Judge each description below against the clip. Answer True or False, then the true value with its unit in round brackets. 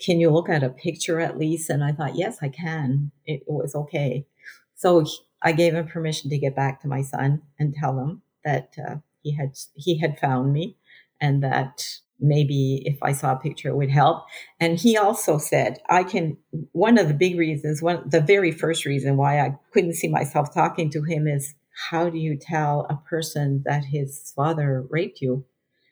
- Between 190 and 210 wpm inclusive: True (200 wpm)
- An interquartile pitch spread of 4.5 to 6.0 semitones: False (2.9 semitones)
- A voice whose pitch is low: False (150 Hz)